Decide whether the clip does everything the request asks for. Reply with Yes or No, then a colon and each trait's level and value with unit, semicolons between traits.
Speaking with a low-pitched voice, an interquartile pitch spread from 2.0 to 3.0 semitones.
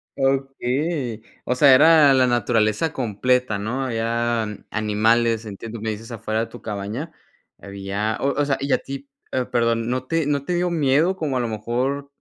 No: low, 125 Hz; average, 3.8 semitones